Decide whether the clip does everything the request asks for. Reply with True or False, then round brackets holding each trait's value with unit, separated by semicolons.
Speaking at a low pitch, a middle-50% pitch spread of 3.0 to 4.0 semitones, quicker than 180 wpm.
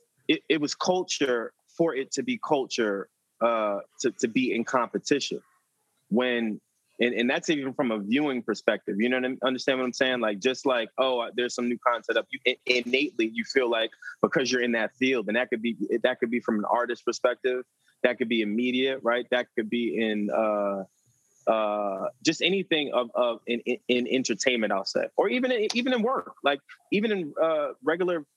True (125 Hz; 3.7 semitones; 205 wpm)